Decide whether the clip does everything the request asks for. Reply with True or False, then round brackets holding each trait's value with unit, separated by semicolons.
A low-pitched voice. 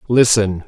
True (105 Hz)